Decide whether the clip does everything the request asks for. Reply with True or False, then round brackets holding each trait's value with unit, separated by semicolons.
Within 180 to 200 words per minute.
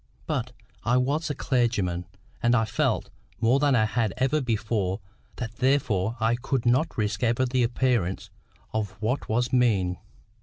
False (160 wpm)